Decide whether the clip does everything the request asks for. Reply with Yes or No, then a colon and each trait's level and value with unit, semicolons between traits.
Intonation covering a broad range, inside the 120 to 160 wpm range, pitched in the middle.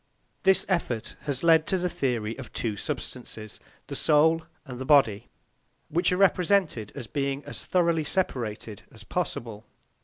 Yes: wide, 6.7 semitones; average, 150 wpm; medium, 145 Hz